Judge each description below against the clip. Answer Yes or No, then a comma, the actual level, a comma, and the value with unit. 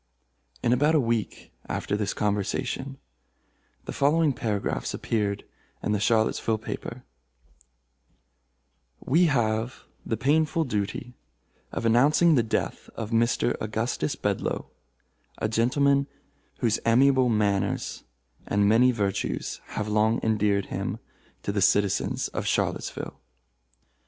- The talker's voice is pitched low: Yes, low, 115 Hz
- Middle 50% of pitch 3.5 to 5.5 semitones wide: Yes, average, 3.9 semitones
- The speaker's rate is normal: No, slow, 110 wpm